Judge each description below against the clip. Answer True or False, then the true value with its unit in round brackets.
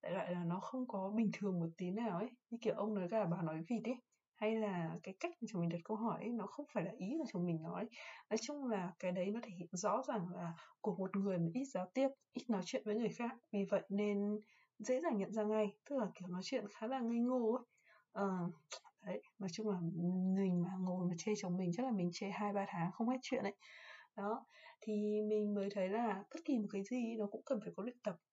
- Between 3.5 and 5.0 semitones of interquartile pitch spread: True (3.8 semitones)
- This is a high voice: True (210 Hz)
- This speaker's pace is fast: True (265 wpm)